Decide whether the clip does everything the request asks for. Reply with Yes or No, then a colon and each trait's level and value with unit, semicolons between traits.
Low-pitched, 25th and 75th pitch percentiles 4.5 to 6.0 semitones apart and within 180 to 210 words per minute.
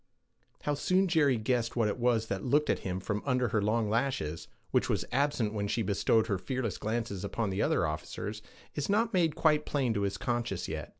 Yes: low, 115 Hz; average, 5.1 semitones; fast, 205 wpm